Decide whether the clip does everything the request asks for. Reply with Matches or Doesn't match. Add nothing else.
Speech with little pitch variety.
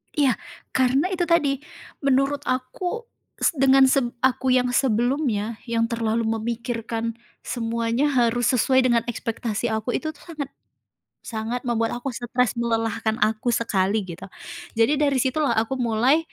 Doesn't match